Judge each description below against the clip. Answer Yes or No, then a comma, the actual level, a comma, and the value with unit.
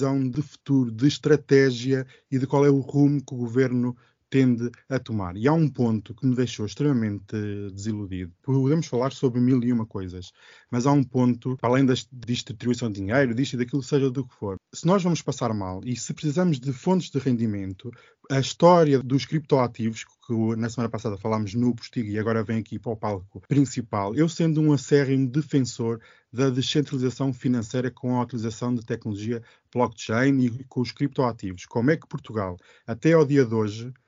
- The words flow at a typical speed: No, fast, 190 wpm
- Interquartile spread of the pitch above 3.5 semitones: No, average, 3.2 semitones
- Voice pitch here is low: Yes, low, 125 Hz